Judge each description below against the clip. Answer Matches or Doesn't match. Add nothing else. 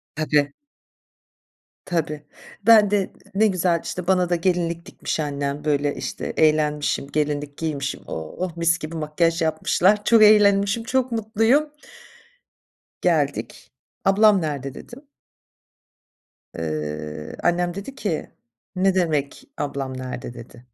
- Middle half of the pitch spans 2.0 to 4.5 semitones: Doesn't match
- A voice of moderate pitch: Matches